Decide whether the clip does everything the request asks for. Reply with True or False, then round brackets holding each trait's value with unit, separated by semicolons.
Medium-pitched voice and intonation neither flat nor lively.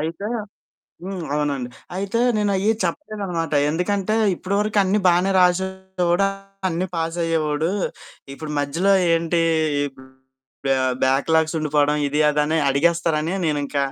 True (165 Hz; 3.9 semitones)